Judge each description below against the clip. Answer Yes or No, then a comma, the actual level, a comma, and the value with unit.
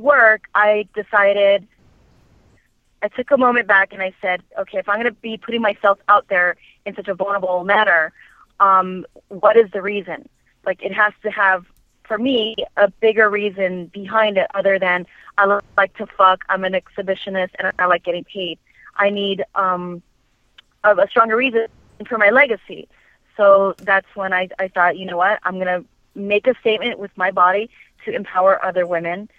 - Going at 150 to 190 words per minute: Yes, average, 180 wpm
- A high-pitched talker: Yes, high, 200 Hz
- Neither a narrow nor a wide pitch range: No, narrow, 2.2 semitones